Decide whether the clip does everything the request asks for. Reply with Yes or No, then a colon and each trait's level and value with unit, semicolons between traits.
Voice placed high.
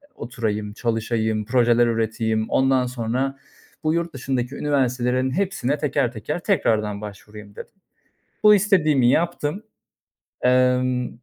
No: low, 125 Hz